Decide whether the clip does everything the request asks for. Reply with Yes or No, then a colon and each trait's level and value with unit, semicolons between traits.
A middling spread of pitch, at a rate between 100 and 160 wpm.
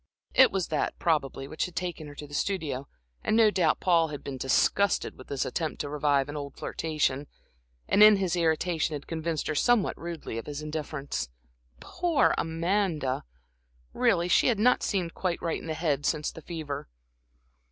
No: average, 3.7 semitones; average, 180 wpm